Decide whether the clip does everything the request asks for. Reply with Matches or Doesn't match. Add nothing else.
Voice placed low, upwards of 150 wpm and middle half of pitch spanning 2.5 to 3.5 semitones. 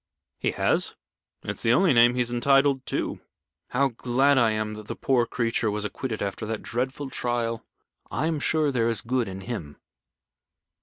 Matches